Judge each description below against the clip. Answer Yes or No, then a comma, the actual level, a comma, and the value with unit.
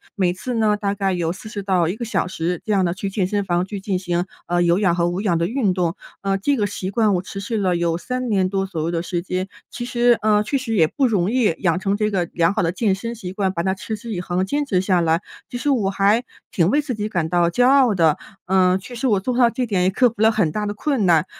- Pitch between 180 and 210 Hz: Yes, high, 195 Hz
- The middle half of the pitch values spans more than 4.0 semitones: No, average, 3.7 semitones